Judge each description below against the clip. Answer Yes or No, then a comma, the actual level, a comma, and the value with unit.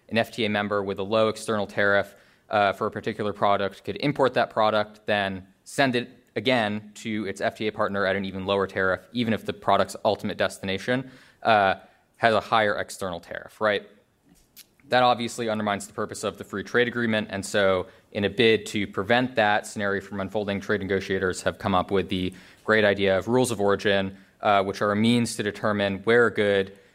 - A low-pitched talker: Yes, low, 105 Hz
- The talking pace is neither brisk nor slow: Yes, average, 195 wpm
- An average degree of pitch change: No, narrow, 2.3 semitones